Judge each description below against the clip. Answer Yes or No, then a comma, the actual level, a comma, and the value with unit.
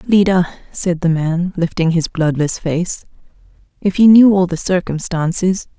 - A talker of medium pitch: Yes, medium, 175 Hz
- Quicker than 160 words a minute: No, average, 145 wpm